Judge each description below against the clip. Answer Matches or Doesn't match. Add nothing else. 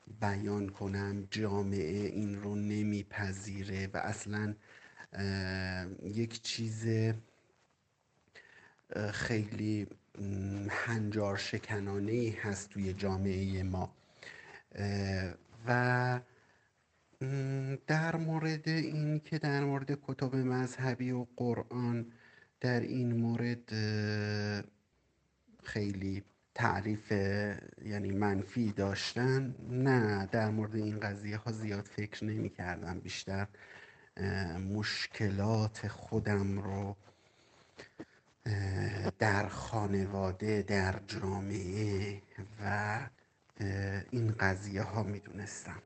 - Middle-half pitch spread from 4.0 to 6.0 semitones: Doesn't match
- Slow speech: Matches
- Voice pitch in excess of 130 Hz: Doesn't match